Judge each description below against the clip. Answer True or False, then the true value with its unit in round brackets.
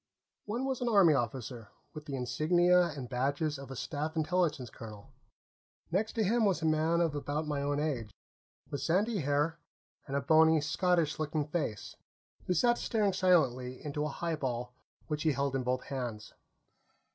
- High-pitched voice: False (150 Hz)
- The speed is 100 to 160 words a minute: False (170 wpm)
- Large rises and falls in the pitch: False (4.3 semitones)